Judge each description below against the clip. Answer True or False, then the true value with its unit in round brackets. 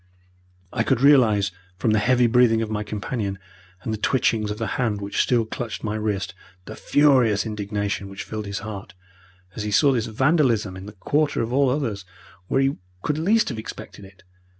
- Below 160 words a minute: False (190 wpm)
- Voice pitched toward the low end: True (110 Hz)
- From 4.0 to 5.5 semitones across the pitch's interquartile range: False (3.6 semitones)